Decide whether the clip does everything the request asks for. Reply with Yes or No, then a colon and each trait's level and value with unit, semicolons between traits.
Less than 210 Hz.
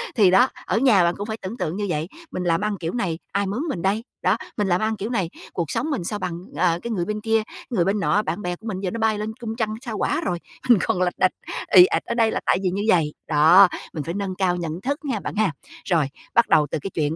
Yes: high, 195 Hz